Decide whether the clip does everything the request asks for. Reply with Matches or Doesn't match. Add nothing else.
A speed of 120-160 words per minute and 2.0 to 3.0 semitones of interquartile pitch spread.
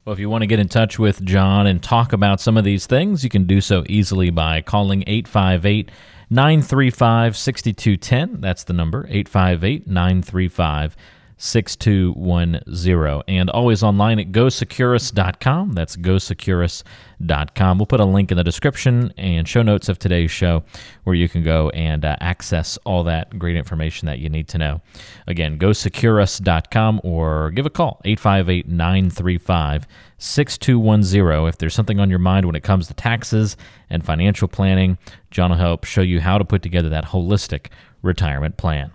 Doesn't match